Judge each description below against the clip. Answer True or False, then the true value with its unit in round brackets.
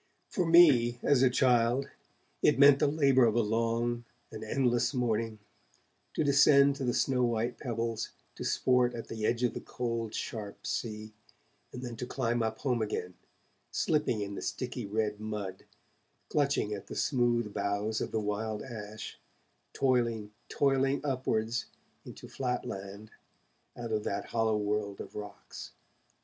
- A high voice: False (115 Hz)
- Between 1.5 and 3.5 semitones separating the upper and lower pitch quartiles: True (2.9 semitones)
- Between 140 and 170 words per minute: True (155 wpm)